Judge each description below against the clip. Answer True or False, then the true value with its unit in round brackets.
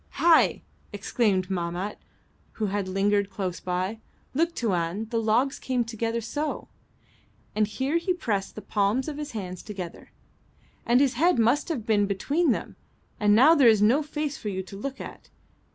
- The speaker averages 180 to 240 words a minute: False (170 wpm)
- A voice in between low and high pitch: False (220 Hz)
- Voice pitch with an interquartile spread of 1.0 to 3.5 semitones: False (5.5 semitones)